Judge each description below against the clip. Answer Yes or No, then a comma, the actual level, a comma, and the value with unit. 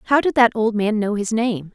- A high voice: Yes, high, 220 Hz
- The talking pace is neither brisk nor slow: No, fast, 275 wpm